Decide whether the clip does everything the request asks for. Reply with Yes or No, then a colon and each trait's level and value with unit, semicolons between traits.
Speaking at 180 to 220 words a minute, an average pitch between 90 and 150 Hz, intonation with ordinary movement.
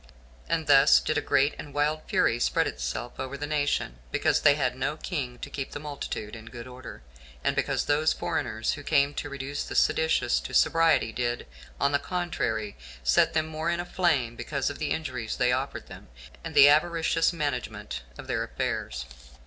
Yes: average, 190 wpm; medium, 140 Hz; average, 4.2 semitones